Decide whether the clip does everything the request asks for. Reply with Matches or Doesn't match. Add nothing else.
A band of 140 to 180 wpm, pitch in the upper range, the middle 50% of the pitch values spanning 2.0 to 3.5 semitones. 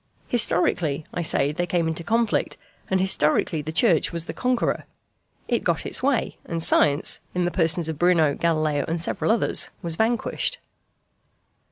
Doesn't match